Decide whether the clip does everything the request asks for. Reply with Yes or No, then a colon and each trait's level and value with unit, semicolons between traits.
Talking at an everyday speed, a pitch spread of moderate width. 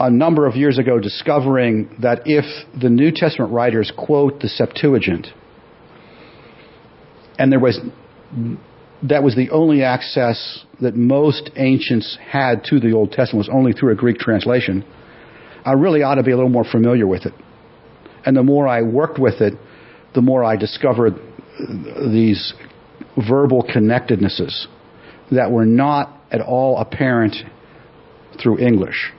Yes: average, 145 wpm; average, 3.3 semitones